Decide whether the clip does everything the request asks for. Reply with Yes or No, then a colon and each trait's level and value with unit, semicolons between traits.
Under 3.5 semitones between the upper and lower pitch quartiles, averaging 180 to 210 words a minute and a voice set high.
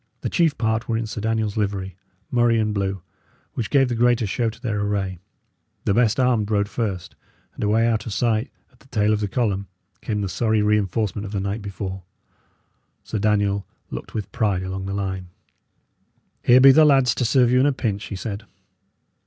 No: average, 2.9 semitones; average, 195 wpm; low, 105 Hz